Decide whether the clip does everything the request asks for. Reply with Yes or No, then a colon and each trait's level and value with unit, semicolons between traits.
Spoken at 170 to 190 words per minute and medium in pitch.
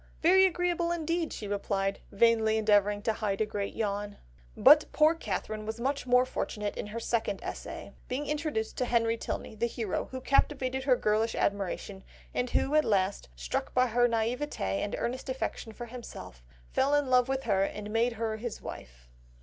No: average, 180 wpm; high, 230 Hz